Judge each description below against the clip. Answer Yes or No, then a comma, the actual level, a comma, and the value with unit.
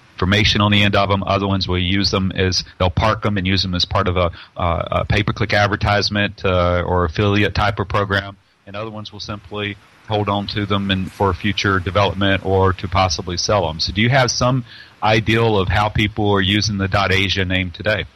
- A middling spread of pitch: No, narrow, 1.6 semitones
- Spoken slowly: No, fast, 215 wpm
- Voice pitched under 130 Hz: Yes, low, 100 Hz